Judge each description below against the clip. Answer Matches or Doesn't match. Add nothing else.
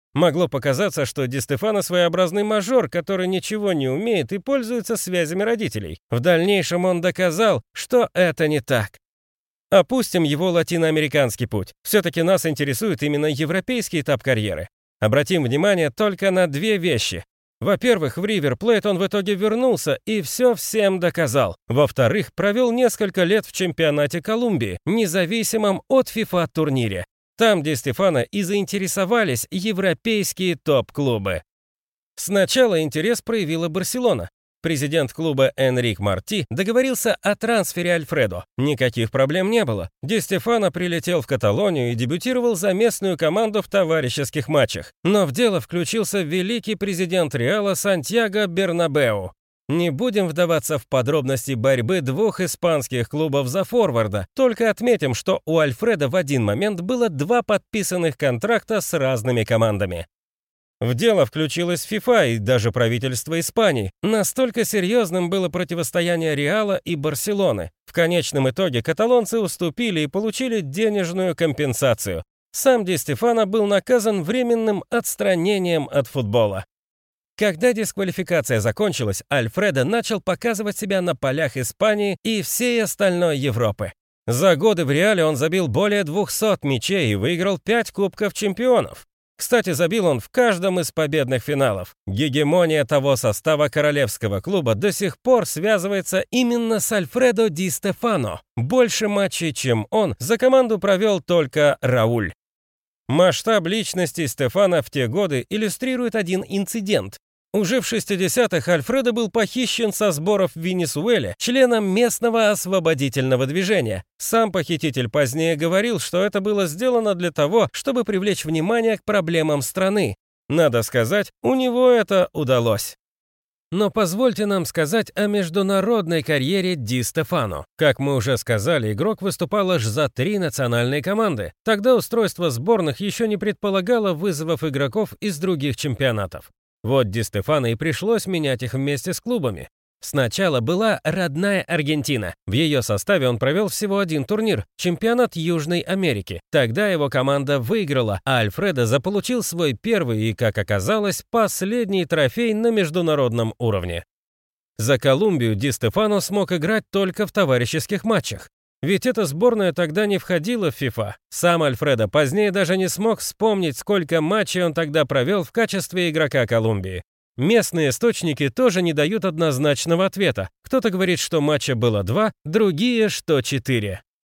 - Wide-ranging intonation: Matches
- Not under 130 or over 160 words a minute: Matches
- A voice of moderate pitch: Matches